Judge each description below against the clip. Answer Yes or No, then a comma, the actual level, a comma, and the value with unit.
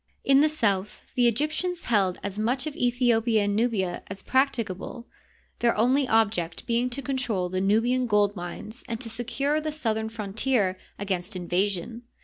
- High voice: Yes, high, 225 Hz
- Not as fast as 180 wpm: Yes, average, 165 wpm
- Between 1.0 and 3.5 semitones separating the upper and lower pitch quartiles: No, average, 4.2 semitones